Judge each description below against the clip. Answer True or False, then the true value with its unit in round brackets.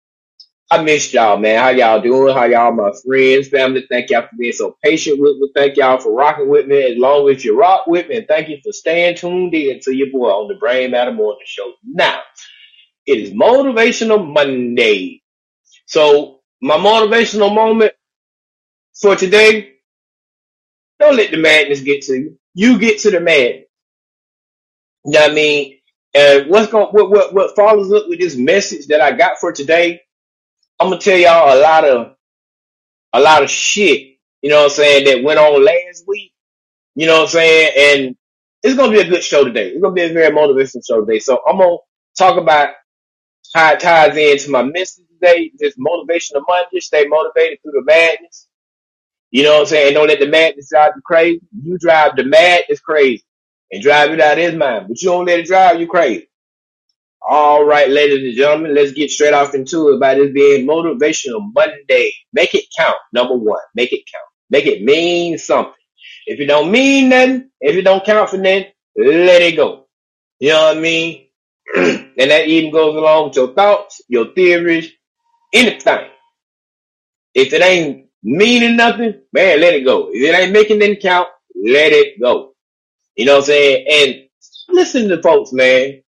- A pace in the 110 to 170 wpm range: False (190 wpm)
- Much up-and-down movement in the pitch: True (7.4 semitones)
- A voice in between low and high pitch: True (170 Hz)